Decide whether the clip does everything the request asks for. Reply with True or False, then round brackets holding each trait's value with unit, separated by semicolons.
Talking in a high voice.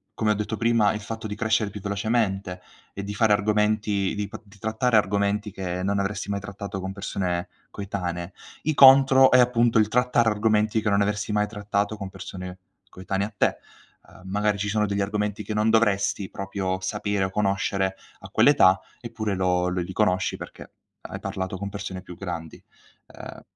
False (100 Hz)